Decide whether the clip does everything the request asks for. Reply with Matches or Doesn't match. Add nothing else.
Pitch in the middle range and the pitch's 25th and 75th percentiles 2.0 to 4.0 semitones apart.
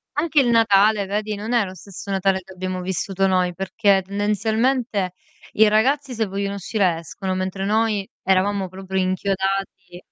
Doesn't match